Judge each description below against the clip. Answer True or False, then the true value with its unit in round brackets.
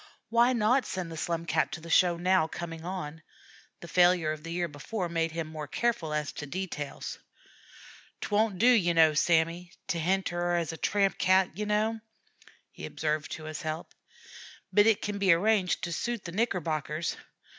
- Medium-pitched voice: True (175 Hz)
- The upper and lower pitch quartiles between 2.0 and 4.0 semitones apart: True (3.6 semitones)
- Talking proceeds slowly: False (185 wpm)